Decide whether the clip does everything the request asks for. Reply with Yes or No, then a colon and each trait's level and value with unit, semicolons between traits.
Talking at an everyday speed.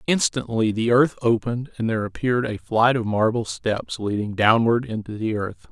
Yes: average, 180 wpm